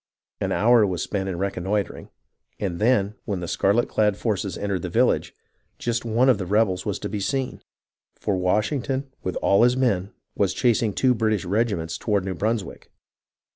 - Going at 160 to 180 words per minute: Yes, average, 175 wpm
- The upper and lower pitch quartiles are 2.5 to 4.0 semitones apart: Yes, average, 3.5 semitones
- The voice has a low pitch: Yes, low, 105 Hz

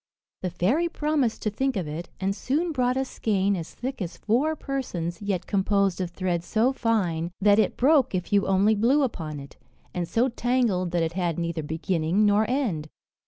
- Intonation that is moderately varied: No, wide, 6.3 semitones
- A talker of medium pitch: No, high, 200 Hz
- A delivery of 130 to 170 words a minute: No, average, 190 wpm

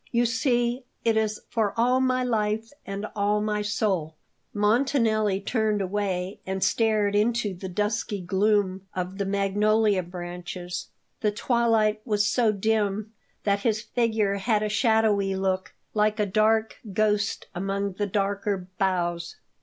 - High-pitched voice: Yes, high, 210 Hz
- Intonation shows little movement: Yes, narrow, 2.2 semitones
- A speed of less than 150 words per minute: Yes, average, 140 wpm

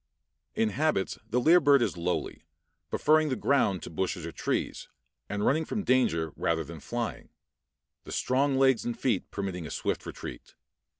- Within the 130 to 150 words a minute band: No, average, 165 wpm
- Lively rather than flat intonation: Yes, wide, 7.6 semitones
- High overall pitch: No, low, 120 Hz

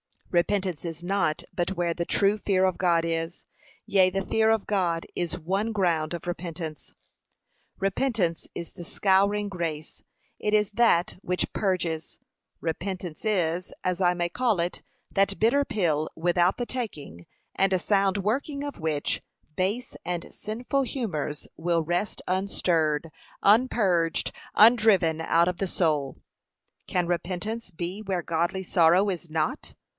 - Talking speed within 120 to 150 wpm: Yes, average, 140 wpm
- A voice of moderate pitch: Yes, medium, 180 Hz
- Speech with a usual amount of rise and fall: Yes, average, 3.3 semitones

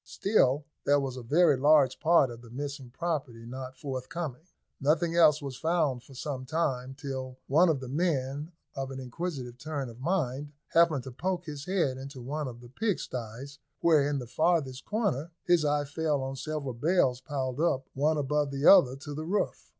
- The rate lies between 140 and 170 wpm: No, average, 185 wpm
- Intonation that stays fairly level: No, average, 3.4 semitones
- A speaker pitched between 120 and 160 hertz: Yes, medium, 140 Hz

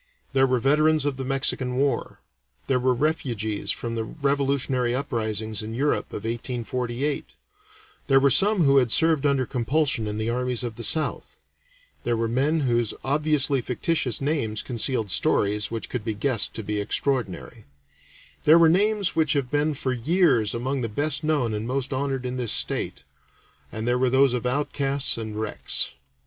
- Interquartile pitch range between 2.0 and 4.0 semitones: Yes, average, 3.7 semitones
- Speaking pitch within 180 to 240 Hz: No, low, 130 Hz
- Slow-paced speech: No, average, 170 wpm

